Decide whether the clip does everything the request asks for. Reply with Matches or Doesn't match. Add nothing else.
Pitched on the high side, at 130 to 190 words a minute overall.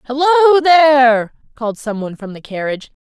Matches